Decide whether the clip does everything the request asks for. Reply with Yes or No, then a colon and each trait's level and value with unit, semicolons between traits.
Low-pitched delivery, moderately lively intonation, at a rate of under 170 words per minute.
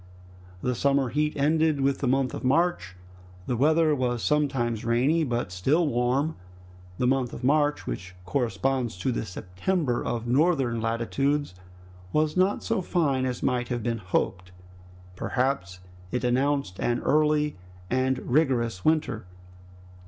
Yes: low, 130 Hz; average, 3.9 semitones; average, 140 wpm